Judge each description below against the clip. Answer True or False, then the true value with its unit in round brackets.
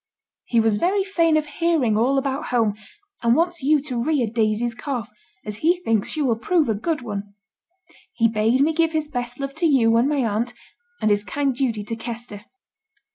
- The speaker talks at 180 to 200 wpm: True (195 wpm)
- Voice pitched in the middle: False (245 Hz)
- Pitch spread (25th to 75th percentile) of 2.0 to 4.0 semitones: False (5.3 semitones)